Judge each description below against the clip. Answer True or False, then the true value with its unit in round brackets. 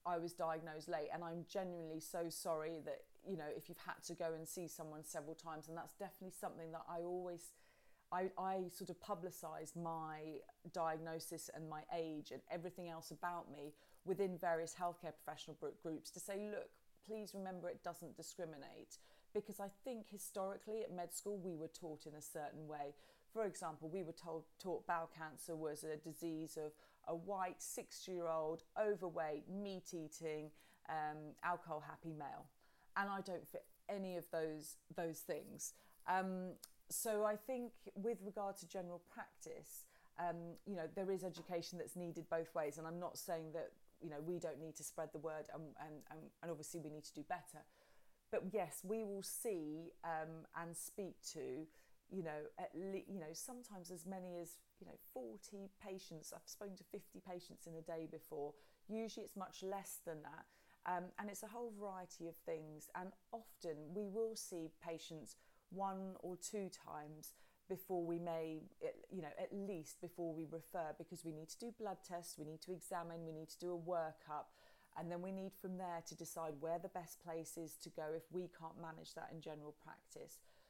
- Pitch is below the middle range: False (170 Hz)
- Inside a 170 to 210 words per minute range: True (185 wpm)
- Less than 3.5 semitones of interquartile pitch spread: True (2.9 semitones)